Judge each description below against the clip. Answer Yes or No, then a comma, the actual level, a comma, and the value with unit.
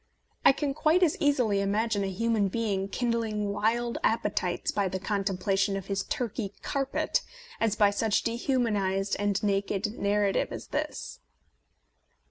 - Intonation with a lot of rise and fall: No, average, 2.8 semitones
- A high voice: Yes, high, 210 Hz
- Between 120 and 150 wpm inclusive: Yes, average, 140 wpm